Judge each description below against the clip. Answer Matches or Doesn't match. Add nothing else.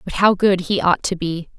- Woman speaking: Matches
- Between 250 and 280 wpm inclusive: Matches